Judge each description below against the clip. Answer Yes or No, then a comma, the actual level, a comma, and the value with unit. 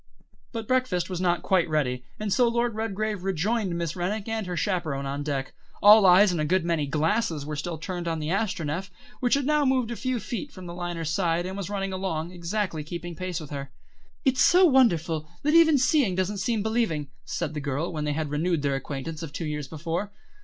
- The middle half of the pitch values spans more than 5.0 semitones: Yes, wide, 5.4 semitones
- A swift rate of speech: Yes, fast, 215 wpm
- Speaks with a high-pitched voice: No, medium, 180 Hz